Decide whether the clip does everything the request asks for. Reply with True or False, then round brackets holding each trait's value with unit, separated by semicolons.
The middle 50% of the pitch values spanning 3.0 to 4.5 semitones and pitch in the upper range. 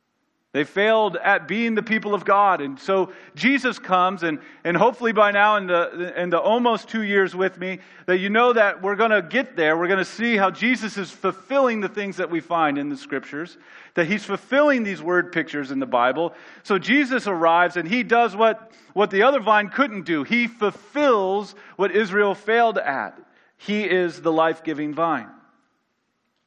True (4.1 semitones; 200 Hz)